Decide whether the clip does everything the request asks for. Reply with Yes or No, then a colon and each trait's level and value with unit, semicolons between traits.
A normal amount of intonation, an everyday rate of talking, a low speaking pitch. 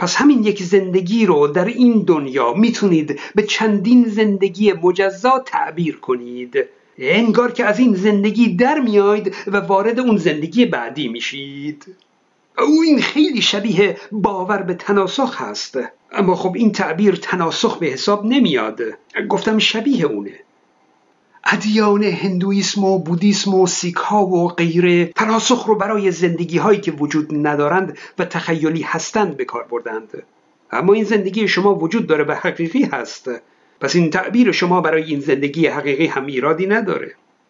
No: average, 4.2 semitones; average, 140 wpm; high, 200 Hz